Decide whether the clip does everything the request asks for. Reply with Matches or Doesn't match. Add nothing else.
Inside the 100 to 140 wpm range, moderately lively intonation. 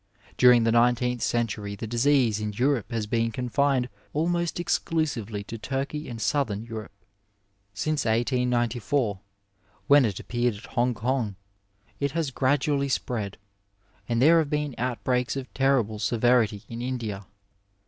Matches